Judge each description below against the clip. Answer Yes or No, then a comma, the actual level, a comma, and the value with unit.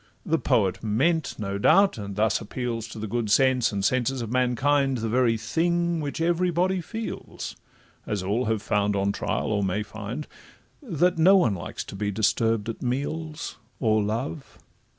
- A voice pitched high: No, low, 120 Hz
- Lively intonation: Yes, wide, 6.8 semitones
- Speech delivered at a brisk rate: No, average, 170 wpm